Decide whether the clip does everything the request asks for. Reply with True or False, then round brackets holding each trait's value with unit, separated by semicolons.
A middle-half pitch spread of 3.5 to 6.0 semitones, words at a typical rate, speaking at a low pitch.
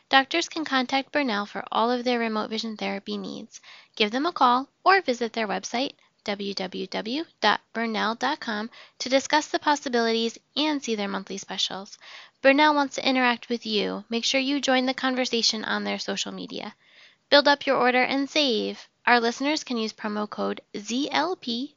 False (4.3 semitones; 165 wpm; 245 Hz)